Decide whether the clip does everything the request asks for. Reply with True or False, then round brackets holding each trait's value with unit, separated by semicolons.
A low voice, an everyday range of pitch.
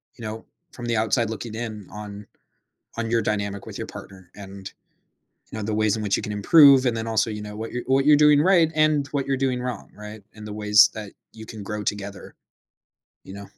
True (110 Hz; 3.1 semitones)